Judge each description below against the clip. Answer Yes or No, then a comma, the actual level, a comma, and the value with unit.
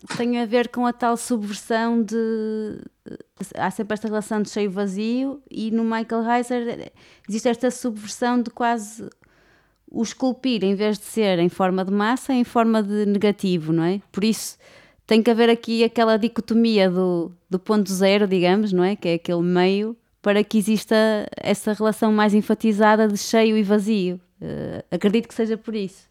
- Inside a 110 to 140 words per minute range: No, average, 175 wpm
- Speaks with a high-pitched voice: Yes, high, 220 Hz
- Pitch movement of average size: No, narrow, 2.3 semitones